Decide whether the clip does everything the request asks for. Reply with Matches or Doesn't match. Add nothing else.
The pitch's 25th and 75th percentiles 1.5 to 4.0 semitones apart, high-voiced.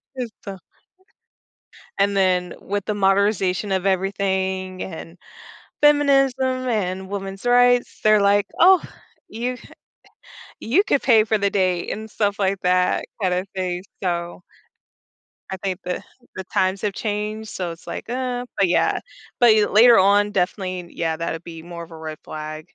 Matches